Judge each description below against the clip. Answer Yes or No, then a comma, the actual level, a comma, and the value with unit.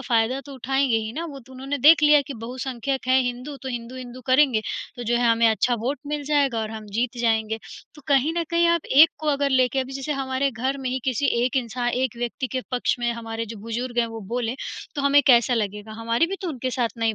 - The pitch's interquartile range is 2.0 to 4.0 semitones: Yes, average, 3.0 semitones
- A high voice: Yes, very high, 255 Hz